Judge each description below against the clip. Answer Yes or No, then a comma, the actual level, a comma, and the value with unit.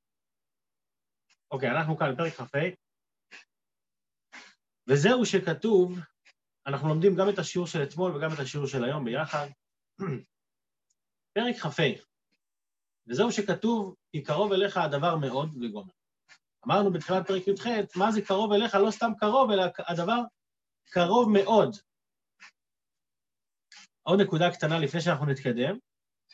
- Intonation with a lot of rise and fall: Yes, wide, 6.1 semitones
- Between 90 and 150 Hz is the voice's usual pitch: No, medium, 175 Hz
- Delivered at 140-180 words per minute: No, average, 120 wpm